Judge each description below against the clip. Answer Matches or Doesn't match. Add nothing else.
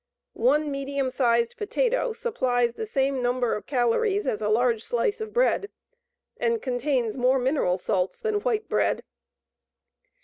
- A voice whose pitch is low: Doesn't match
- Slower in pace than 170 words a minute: Matches